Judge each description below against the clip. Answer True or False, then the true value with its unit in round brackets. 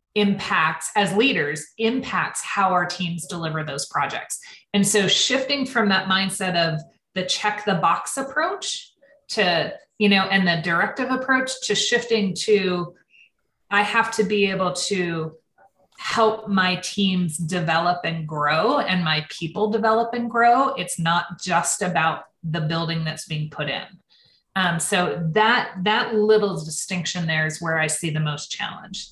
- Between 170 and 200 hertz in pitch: True (190 Hz)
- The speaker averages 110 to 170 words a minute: True (150 wpm)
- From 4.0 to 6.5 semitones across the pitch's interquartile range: True (4.4 semitones)